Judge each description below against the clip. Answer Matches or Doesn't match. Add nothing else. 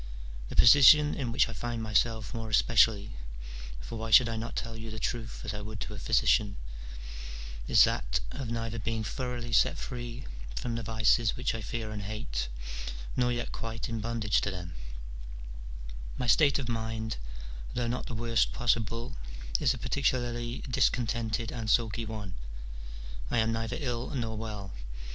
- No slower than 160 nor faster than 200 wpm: Matches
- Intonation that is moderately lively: Doesn't match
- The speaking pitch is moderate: Doesn't match